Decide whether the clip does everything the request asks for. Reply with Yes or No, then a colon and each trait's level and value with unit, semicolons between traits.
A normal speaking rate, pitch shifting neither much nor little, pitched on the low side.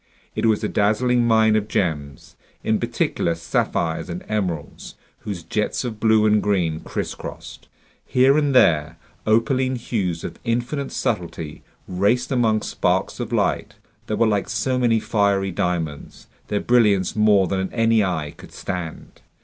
Yes: average, 145 wpm; average, 4.6 semitones; low, 105 Hz